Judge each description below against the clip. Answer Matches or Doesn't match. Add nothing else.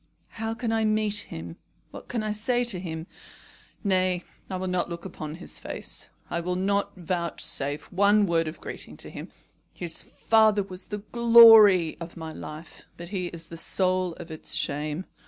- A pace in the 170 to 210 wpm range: Matches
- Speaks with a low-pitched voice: Doesn't match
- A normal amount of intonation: Matches